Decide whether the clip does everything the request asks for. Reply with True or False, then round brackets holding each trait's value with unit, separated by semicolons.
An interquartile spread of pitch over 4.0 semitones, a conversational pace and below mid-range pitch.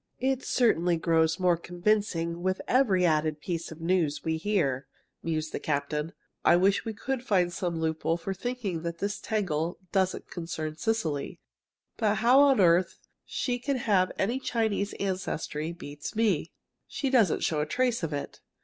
False (5.1 semitones; 160 wpm; 180 Hz)